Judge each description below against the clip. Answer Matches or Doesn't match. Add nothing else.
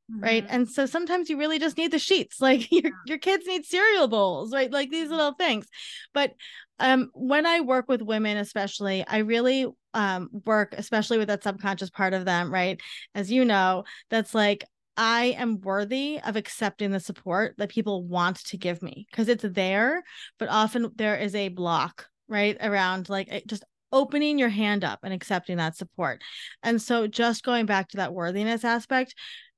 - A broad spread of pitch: Doesn't match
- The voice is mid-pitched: Doesn't match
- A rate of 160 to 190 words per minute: Matches